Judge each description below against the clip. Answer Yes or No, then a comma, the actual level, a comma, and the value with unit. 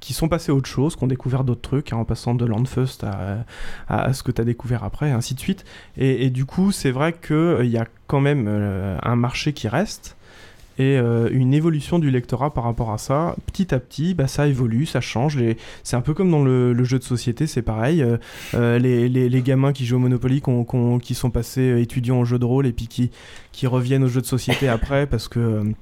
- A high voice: No, low, 125 Hz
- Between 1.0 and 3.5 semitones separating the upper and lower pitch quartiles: Yes, narrow, 2.5 semitones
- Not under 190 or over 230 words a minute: No, fast, 260 wpm